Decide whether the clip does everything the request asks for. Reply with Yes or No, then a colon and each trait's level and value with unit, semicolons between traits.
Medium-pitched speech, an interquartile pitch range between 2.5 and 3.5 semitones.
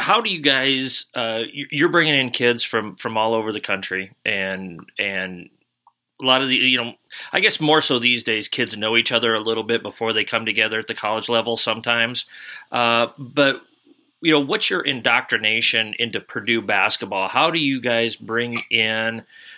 No: low, 115 Hz; average, 2.8 semitones